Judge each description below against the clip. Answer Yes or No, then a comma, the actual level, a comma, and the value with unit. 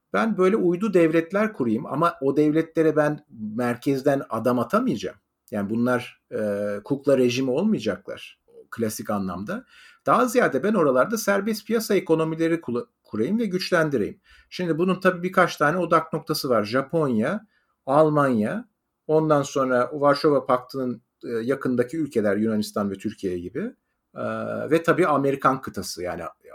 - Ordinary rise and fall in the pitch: No, wide, 6.1 semitones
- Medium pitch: Yes, medium, 150 Hz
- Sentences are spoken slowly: No, average, 130 wpm